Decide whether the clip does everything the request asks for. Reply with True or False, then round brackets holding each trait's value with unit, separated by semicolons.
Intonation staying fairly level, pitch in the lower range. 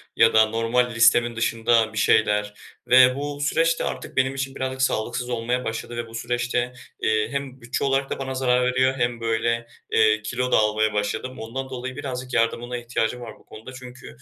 True (2.3 semitones; 120 Hz)